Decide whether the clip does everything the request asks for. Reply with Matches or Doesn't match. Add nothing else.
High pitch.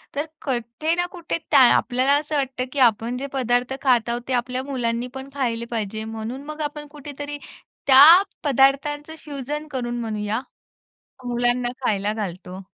Matches